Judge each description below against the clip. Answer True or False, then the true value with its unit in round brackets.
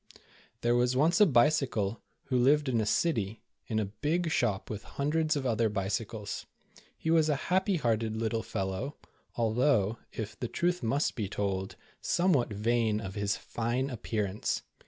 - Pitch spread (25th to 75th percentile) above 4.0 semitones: True (5.5 semitones)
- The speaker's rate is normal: True (155 wpm)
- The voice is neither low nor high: False (120 Hz)